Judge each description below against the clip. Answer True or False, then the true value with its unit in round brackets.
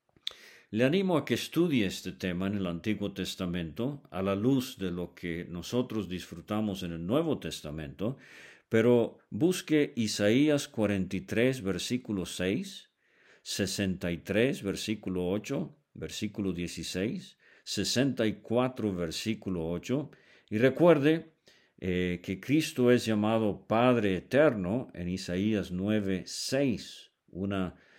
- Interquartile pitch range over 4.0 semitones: True (5.2 semitones)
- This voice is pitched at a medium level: False (100 Hz)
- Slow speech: True (110 wpm)